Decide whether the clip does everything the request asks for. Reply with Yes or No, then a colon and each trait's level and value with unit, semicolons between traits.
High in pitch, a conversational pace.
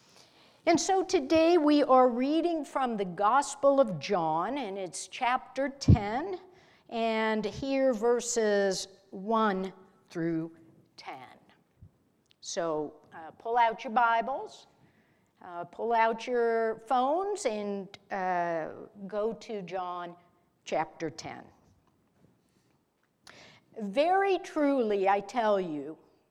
No: high, 225 Hz; slow, 100 wpm